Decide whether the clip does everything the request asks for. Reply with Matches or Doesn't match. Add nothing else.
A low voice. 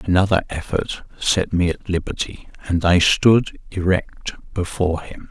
Matches